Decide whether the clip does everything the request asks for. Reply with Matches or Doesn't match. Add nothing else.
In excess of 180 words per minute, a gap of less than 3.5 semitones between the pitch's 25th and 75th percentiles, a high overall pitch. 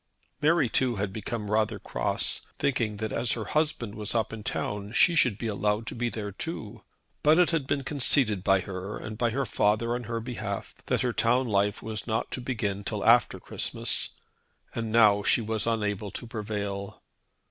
Doesn't match